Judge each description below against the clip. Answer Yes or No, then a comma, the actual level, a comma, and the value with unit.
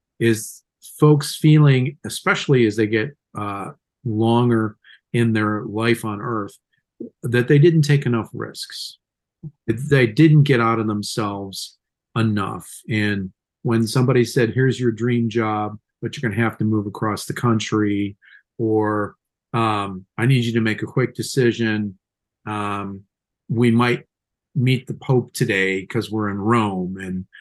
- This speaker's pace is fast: No, average, 145 wpm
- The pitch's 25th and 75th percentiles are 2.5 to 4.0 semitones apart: Yes, average, 2.9 semitones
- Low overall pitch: Yes, low, 115 Hz